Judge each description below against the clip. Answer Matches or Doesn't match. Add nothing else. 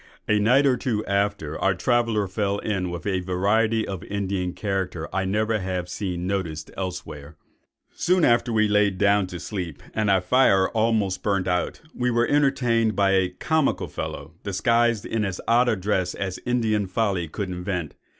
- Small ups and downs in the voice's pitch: Doesn't match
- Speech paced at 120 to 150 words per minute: Doesn't match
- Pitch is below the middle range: Matches